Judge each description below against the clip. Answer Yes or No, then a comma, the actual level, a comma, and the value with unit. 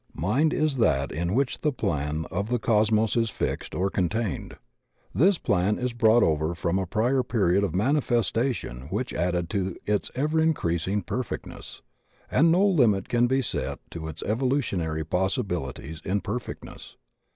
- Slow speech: No, average, 155 wpm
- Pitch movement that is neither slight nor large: No, wide, 6.3 semitones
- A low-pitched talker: Yes, low, 105 Hz